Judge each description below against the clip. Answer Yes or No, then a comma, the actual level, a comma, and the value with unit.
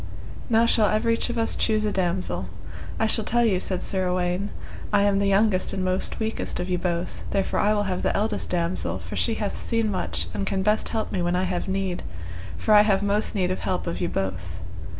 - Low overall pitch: No, high, 195 Hz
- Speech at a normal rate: No, fast, 225 wpm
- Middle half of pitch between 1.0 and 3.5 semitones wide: Yes, average, 2.9 semitones